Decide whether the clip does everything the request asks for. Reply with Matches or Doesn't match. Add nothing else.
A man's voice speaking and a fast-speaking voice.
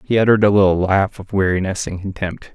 Matches